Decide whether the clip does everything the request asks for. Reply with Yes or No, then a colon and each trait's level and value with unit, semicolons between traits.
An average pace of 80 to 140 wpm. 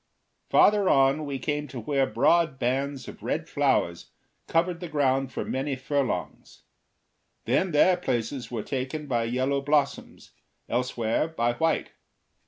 Yes: slow, 135 wpm